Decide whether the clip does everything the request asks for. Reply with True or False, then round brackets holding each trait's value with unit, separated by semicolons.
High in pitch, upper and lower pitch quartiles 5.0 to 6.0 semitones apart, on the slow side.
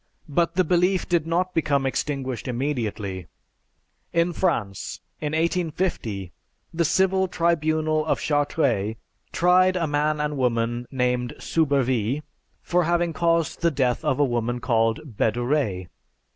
False (150 Hz; 5.6 semitones; 125 wpm)